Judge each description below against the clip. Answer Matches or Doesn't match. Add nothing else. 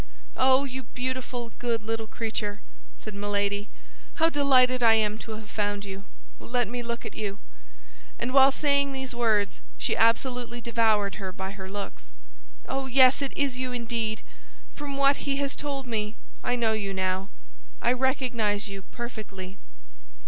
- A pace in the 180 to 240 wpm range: Doesn't match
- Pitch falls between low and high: Doesn't match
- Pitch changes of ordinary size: Matches